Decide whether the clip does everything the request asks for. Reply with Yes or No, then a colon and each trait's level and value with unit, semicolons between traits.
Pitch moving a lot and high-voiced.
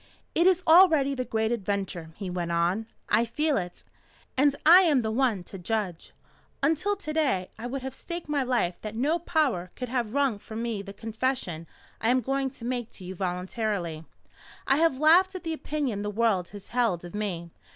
Yes: wide, 6.4 semitones; high, 235 Hz